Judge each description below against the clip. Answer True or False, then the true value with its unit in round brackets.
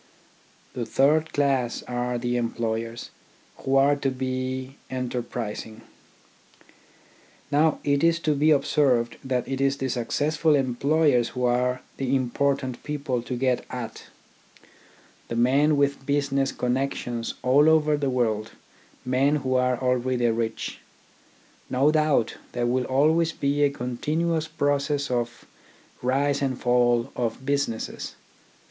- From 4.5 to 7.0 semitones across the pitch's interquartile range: False (2.7 semitones)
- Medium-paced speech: False (130 wpm)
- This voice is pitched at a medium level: False (130 Hz)